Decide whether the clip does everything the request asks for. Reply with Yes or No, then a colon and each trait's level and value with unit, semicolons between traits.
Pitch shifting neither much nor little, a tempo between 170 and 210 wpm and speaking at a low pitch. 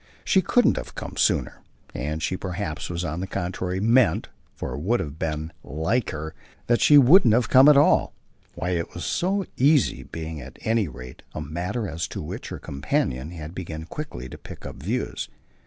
No: wide, 7.6 semitones; average, 190 wpm; very low, 90 Hz